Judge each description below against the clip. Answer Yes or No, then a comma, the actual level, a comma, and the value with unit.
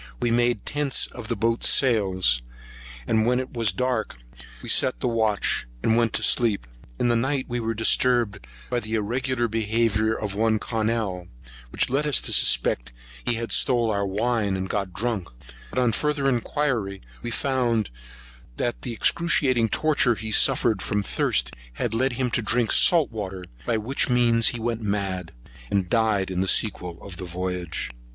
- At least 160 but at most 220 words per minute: Yes, average, 170 wpm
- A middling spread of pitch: Yes, average, 3.3 semitones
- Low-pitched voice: Yes, low, 115 Hz